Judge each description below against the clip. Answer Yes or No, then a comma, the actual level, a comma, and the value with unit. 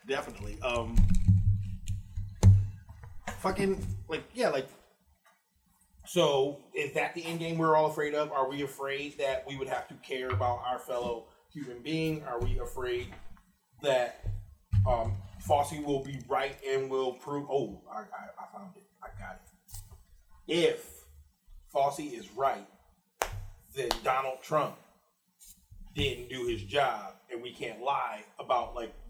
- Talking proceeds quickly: No, average, 140 wpm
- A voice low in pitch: Yes, low, 120 Hz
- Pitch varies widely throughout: Yes, wide, 6.5 semitones